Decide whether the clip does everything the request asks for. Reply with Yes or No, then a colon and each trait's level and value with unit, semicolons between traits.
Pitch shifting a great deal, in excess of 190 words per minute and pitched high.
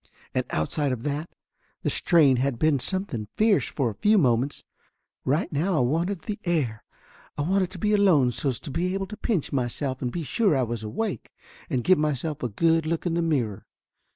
No: wide, 6.1 semitones; average, 200 wpm; medium, 155 Hz